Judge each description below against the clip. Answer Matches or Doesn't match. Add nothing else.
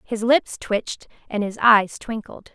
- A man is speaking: Doesn't match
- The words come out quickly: Doesn't match